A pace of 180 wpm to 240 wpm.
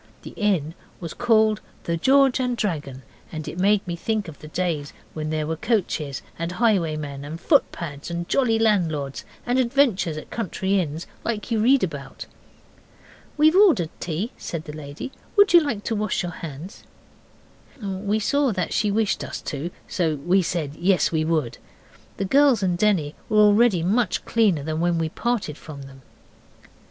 No: average, 170 wpm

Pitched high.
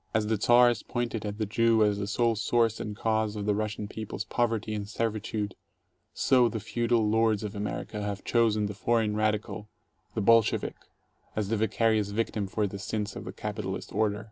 No: low, 110 Hz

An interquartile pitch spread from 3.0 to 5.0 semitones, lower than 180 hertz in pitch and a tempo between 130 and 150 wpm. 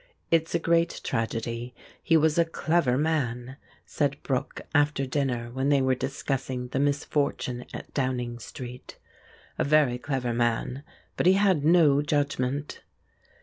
Yes: average, 3.3 semitones; low, 135 Hz; average, 140 wpm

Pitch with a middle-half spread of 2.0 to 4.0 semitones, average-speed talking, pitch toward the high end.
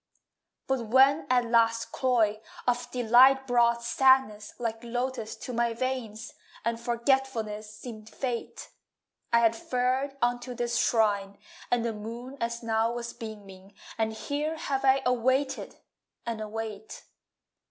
No: narrow, 2.5 semitones; slow, 130 wpm; high, 235 Hz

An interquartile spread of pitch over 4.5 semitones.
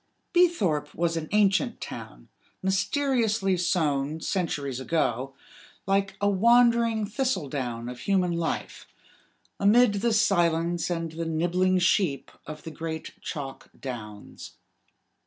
Yes: average, 5.0 semitones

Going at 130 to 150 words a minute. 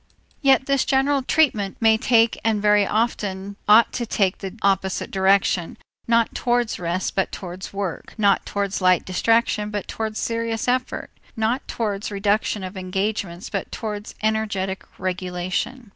Yes: average, 145 wpm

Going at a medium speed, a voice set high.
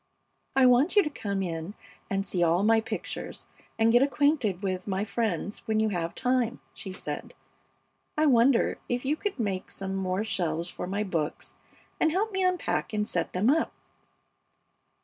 Yes: average, 170 wpm; high, 215 Hz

